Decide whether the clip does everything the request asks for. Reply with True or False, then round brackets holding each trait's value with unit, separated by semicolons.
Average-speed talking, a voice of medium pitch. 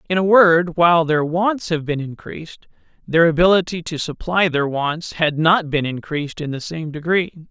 True (185 wpm; 165 Hz)